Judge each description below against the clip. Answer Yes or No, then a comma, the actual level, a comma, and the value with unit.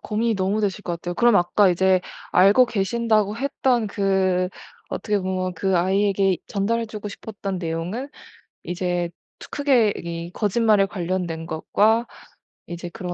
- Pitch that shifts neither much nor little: Yes, average, 3.2 semitones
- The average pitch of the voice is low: No, high, 195 Hz